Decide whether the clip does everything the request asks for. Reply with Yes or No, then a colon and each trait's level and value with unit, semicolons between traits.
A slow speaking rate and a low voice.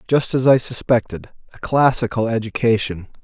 Yes: slow, 110 wpm; low, 115 Hz